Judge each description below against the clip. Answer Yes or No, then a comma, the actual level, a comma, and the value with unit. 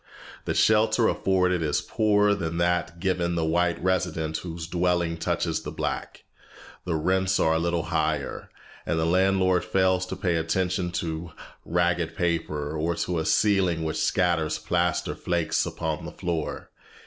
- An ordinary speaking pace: Yes, average, 150 wpm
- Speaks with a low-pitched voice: Yes, very low, 85 Hz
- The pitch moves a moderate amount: No, narrow, 2.2 semitones